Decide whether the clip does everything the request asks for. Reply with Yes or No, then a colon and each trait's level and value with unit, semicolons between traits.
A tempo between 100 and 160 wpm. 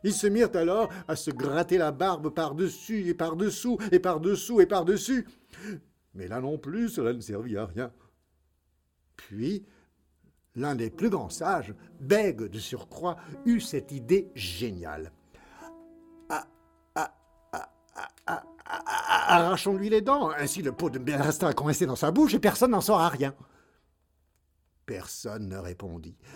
Yes: average, 155 wpm